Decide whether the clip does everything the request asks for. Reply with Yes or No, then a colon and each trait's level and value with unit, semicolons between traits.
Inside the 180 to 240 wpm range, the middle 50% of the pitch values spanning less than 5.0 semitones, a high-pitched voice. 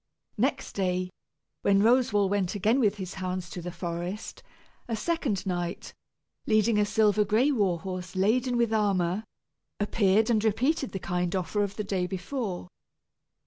No: average, 150 wpm; average, 3.1 semitones; high, 200 Hz